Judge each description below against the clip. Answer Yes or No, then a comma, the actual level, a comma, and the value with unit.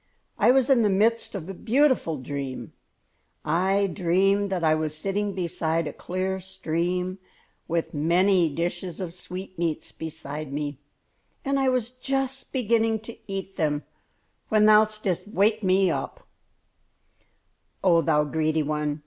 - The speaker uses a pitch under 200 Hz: Yes, medium, 185 Hz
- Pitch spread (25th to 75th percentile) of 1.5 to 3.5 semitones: No, average, 4.8 semitones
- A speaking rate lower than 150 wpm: Yes, slow, 135 wpm